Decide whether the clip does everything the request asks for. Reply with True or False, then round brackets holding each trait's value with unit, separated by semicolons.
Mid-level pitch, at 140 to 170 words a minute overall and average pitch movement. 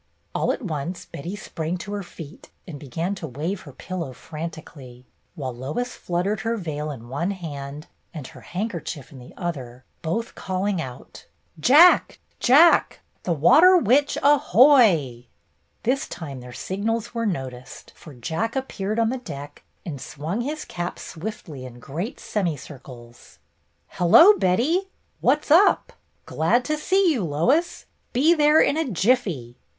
False (175 Hz; 150 wpm; 8.6 semitones)